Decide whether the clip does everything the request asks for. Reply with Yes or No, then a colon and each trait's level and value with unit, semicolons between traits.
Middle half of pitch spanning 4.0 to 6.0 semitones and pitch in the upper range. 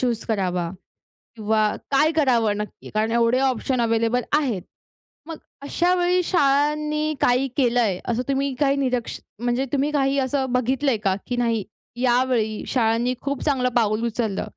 No: average, 3.5 semitones; very high, 250 Hz